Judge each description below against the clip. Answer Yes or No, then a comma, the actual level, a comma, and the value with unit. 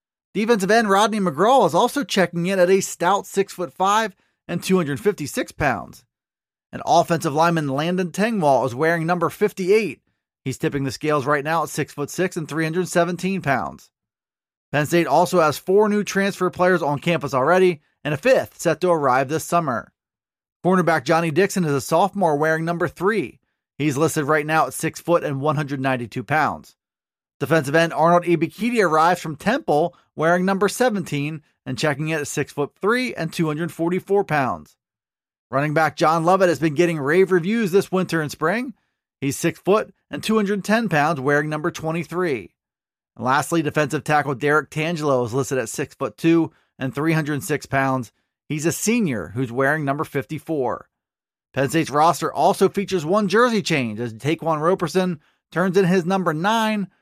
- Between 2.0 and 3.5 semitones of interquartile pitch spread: No, average, 4.0 semitones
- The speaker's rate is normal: Yes, average, 155 wpm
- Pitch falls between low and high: Yes, medium, 165 Hz